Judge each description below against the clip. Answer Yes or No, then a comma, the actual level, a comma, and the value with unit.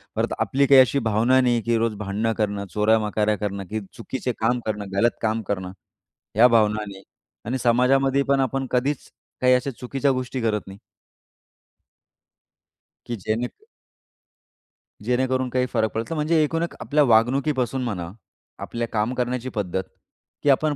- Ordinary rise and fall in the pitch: Yes, average, 3.4 semitones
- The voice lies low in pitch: Yes, low, 120 Hz